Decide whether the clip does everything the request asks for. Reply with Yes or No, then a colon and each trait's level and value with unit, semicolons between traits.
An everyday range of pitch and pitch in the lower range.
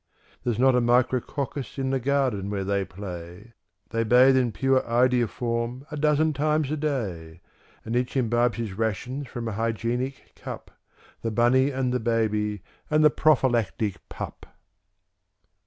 Yes: average, 3.2 semitones; low, 120 Hz